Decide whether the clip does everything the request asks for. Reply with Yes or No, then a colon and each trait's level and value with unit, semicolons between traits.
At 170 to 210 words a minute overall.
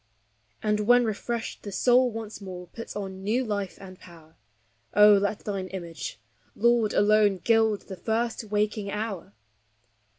No: average, 140 wpm